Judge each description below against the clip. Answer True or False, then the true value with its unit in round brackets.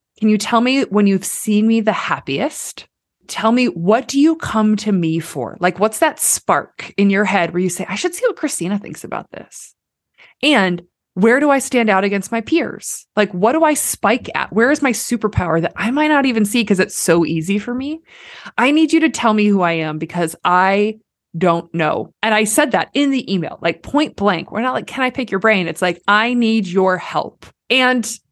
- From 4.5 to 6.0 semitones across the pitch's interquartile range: True (5.4 semitones)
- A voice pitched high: True (215 Hz)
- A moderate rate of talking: False (225 wpm)